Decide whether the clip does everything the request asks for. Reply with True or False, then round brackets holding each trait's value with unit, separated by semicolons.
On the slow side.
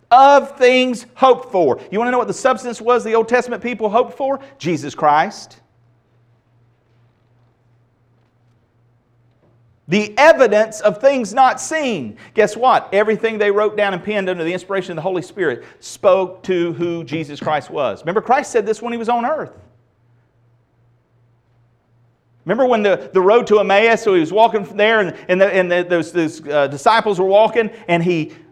False (175 wpm)